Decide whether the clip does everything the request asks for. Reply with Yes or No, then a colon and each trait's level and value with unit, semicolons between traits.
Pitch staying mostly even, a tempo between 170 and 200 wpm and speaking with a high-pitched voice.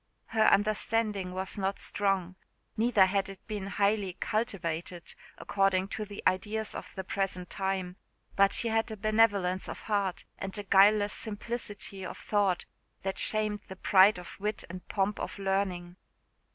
No: narrow, 2.0 semitones; average, 150 wpm; high, 195 Hz